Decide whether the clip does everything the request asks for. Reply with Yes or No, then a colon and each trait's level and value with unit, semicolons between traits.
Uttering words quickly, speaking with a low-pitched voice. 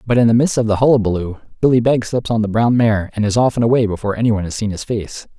Yes: fast, 280 wpm; low, 110 Hz